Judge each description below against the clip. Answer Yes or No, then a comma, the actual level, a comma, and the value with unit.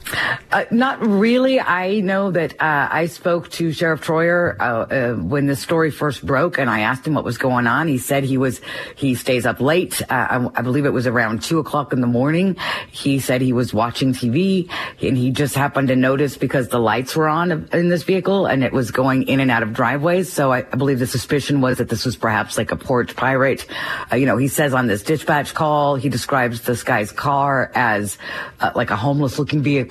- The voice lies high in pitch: No, medium, 140 Hz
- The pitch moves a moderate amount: Yes, average, 4.1 semitones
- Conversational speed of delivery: No, fast, 225 wpm